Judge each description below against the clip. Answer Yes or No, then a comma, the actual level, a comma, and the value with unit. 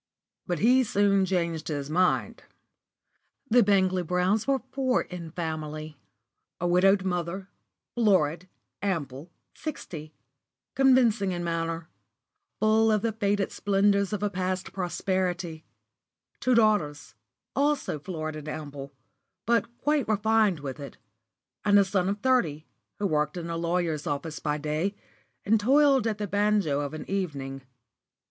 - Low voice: No, medium, 185 Hz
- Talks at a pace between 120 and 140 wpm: Yes, slow, 135 wpm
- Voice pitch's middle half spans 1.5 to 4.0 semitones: No, average, 4.9 semitones